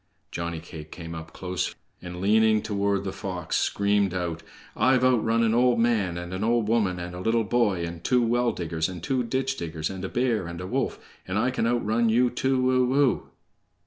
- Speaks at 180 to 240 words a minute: Yes, fast, 205 wpm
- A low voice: Yes, low, 105 Hz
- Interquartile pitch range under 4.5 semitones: No, average, 5.2 semitones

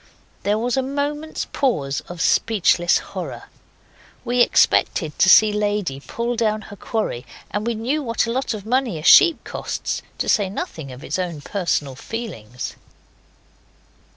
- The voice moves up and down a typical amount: No, wide, 5.8 semitones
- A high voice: Yes, high, 215 Hz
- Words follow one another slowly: No, average, 155 wpm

